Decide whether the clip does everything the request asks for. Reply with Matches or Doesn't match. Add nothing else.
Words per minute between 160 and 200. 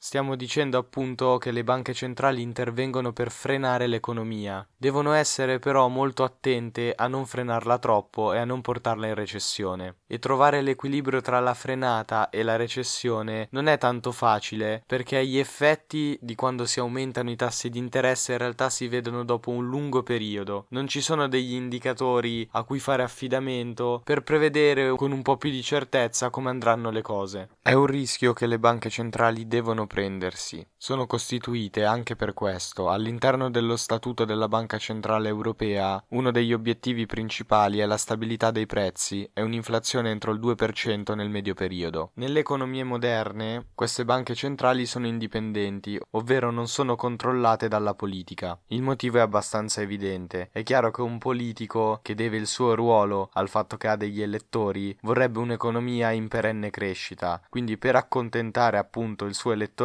Matches